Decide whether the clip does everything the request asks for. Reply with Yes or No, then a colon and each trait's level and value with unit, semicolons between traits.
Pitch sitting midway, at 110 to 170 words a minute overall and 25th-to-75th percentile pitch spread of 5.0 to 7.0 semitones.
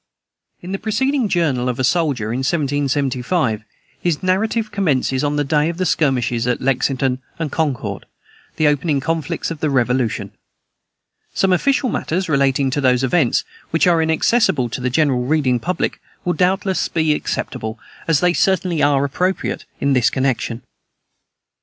Yes: medium, 145 Hz; average, 155 wpm; average, 5.3 semitones